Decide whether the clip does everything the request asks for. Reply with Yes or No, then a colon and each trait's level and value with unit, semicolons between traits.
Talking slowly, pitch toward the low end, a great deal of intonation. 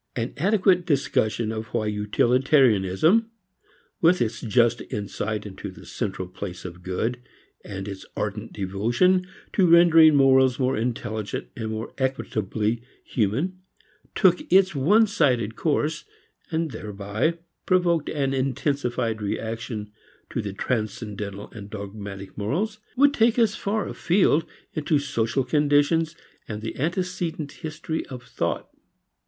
Yes: slow, 120 wpm; low, 125 Hz; wide, 7.5 semitones